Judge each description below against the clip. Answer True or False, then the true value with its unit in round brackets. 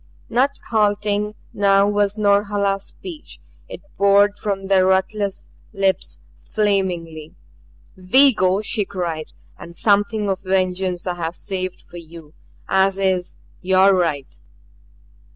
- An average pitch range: False (2.0 semitones)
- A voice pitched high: True (195 Hz)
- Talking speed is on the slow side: True (115 wpm)